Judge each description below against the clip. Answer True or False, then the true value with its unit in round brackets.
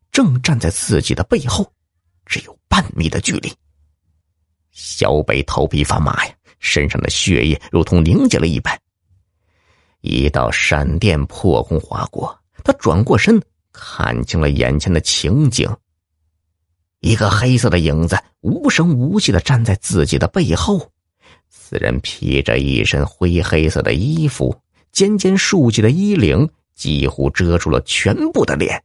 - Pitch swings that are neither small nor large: False (6.3 semitones)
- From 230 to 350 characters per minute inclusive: False (210 characters per minute)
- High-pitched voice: False (85 Hz)